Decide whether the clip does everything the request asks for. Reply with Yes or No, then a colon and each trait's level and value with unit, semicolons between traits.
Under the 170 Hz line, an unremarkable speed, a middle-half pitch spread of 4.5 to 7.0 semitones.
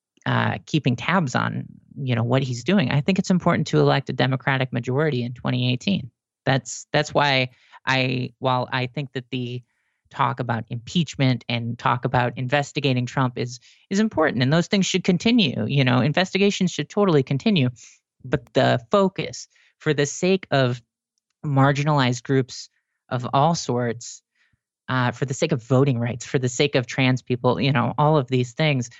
No: low, 135 Hz; average, 170 wpm; average, 3.7 semitones